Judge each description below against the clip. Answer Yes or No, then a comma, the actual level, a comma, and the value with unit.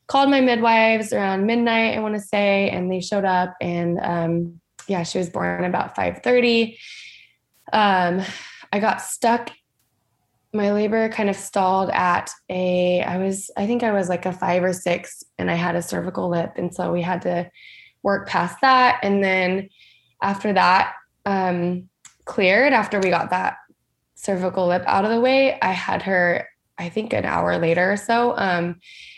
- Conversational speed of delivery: Yes, average, 175 wpm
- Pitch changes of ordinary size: Yes, average, 3.2 semitones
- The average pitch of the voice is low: No, high, 190 Hz